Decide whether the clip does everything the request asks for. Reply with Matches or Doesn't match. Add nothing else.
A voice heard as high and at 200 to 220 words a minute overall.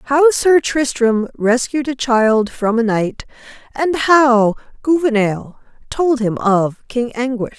Doesn't match